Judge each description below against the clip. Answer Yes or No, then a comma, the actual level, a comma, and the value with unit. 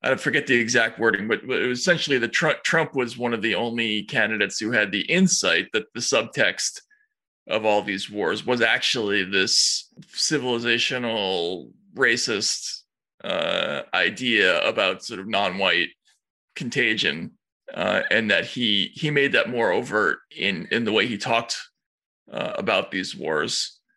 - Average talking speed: Yes, average, 150 wpm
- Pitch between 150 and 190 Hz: No, low, 125 Hz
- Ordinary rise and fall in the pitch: No, wide, 6.9 semitones